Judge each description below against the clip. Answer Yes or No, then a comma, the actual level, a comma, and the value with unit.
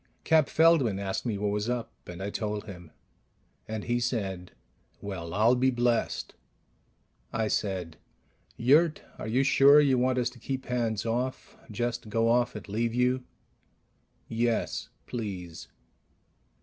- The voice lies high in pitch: No, low, 115 Hz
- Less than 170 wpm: Yes, average, 140 wpm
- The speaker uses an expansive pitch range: No, average, 3.4 semitones